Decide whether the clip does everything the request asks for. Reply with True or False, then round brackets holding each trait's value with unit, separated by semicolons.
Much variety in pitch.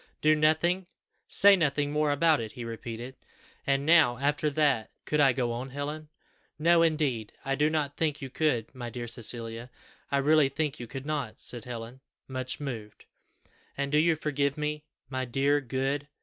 False (3.6 semitones)